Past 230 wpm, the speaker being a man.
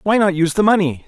Yes: fast, 280 wpm; male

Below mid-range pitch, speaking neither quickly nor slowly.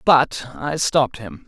Yes: low, 130 Hz; average, 160 wpm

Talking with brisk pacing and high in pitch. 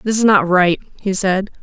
Yes: fast, 220 wpm; high, 195 Hz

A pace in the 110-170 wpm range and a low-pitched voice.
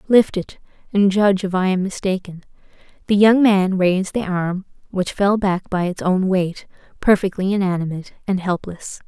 No: average, 165 wpm; high, 190 Hz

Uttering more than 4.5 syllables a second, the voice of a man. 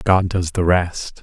No: 3.5 syllables/s; male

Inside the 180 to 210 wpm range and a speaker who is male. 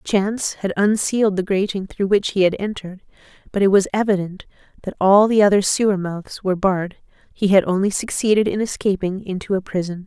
No: average, 185 wpm; female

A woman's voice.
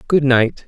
No: male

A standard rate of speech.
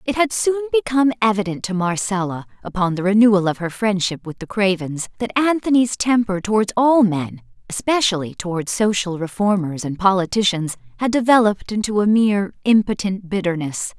Yes: average, 150 wpm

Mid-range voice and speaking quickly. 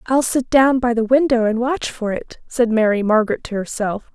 No: high, 235 Hz; fast, 215 wpm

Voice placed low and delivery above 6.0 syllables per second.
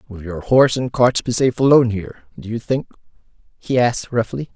Yes: low, 120 Hz; 6.3 syllables/s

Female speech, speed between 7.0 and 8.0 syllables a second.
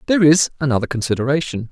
No: male; 7.6 syllables/s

